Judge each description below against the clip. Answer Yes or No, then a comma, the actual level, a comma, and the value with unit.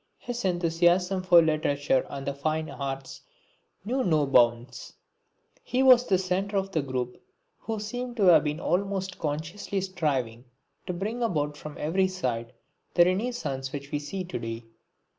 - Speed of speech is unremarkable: Yes, average, 155 wpm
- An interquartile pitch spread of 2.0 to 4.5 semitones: No, wide, 5.5 semitones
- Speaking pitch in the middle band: Yes, medium, 165 Hz